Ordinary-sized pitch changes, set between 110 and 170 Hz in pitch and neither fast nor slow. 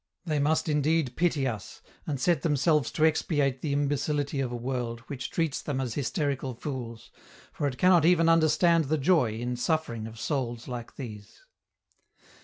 Yes: average, 4.3 semitones; medium, 140 Hz; average, 165 wpm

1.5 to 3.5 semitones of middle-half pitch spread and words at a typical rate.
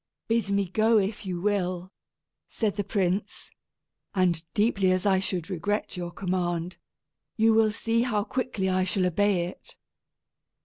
Yes: narrow, 2.4 semitones; average, 145 wpm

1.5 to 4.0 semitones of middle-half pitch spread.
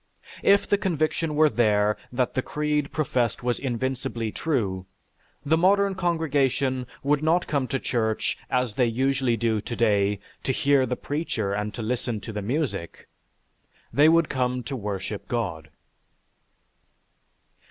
No: average, 5.1 semitones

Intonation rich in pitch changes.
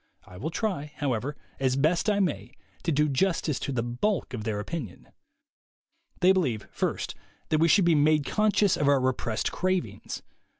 Yes: wide, 6.0 semitones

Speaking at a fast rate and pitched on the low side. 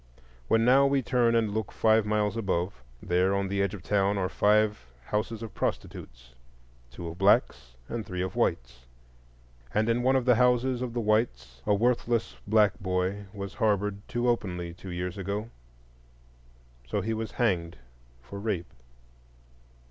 No: average, 155 wpm; low, 105 Hz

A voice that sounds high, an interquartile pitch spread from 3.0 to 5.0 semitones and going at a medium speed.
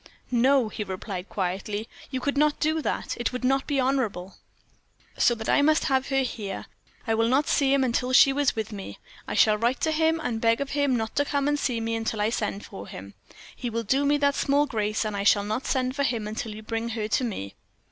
No: high, 240 Hz; average, 4.5 semitones; fast, 240 wpm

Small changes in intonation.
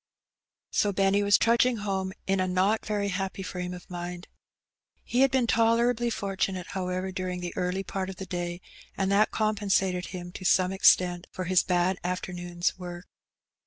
Yes: narrow, 2.0 semitones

